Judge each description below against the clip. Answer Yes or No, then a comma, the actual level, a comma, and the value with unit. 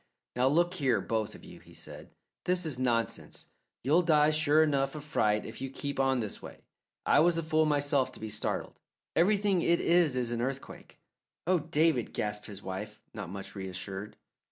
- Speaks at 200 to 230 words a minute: No, average, 185 wpm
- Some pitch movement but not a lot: No, wide, 6.5 semitones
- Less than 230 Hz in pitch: Yes, low, 135 Hz